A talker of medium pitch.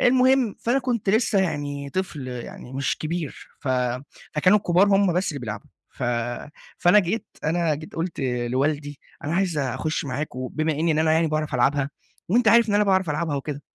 Yes: medium, 155 Hz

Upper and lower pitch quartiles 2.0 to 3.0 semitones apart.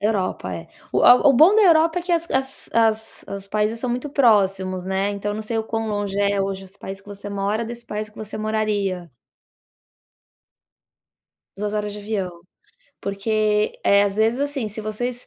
Yes: narrow, 2.5 semitones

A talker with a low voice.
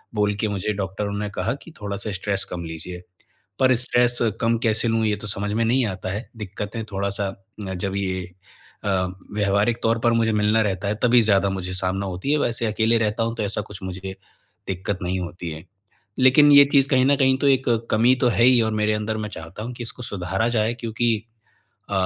Yes: low, 105 Hz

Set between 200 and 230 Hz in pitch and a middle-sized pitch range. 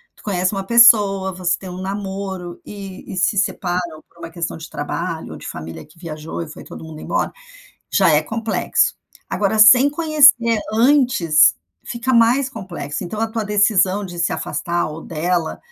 No: high, 190 Hz; average, 4.5 semitones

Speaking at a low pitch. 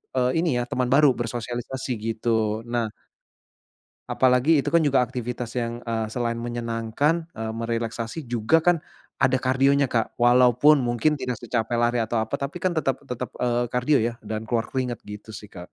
Yes: low, 120 Hz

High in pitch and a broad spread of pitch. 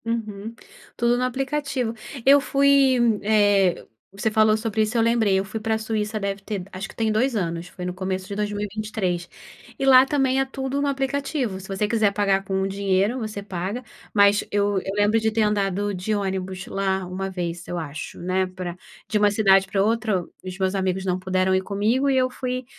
No: high, 205 Hz; average, 3.2 semitones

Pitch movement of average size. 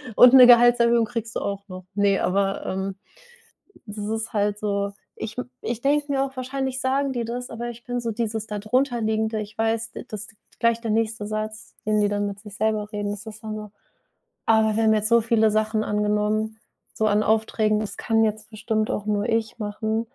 No: narrow, 1.8 semitones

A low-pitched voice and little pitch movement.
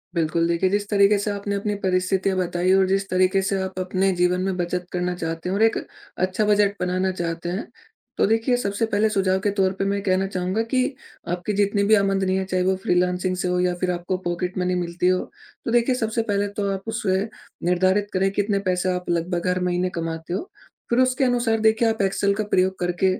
No: high, 190 Hz; narrow, 2.0 semitones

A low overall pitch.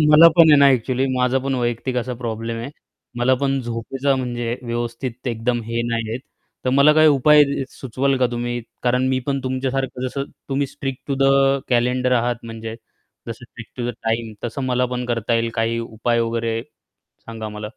Yes: low, 125 Hz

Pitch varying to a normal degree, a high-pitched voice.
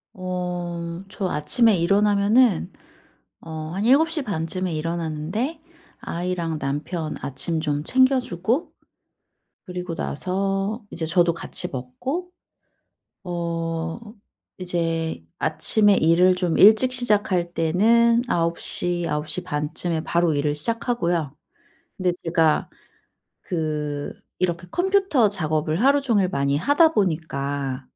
No: average, 4.6 semitones; medium, 175 Hz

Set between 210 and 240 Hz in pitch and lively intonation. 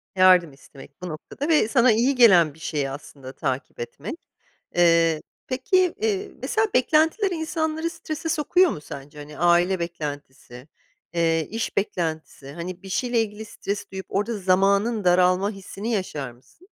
No: medium, 185 Hz; wide, 8.0 semitones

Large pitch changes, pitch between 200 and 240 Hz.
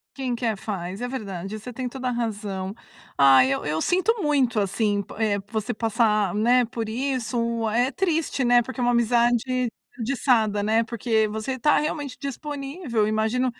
No: average, 3.2 semitones; high, 235 Hz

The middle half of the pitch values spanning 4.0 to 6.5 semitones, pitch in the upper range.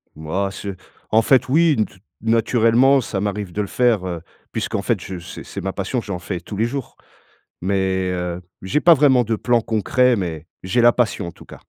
No: average, 4.6 semitones; low, 105 Hz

